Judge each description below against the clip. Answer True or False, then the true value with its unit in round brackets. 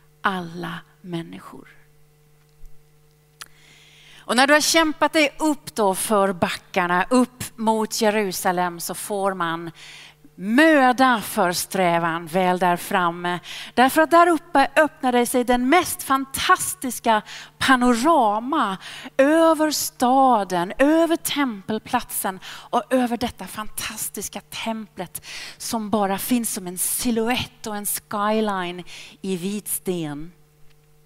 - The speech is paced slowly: True (105 wpm)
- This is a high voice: True (210 Hz)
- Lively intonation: True (6.5 semitones)